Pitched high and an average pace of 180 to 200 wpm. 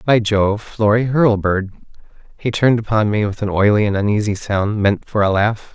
No: low, 105 Hz; average, 190 wpm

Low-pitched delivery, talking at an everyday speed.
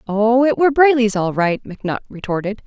No: high, 225 Hz; average, 180 wpm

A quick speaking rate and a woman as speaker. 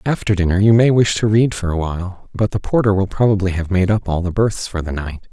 No: fast, 270 wpm; male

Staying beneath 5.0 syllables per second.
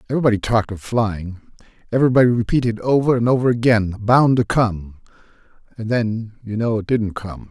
No: 5.8 syllables/s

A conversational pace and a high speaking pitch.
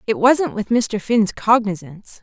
Yes: average, 160 wpm; high, 215 Hz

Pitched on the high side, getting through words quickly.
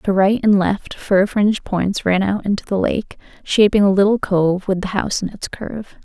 Yes: high, 200 Hz; fast, 220 wpm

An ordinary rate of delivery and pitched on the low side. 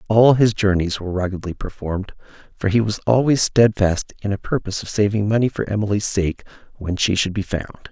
Yes: average, 190 wpm; low, 105 Hz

